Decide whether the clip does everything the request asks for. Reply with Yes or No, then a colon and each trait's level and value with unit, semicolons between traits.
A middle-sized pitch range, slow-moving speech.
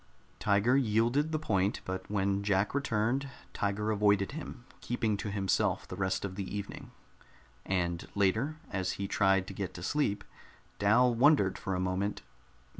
No: average, 3.6 semitones; average, 155 wpm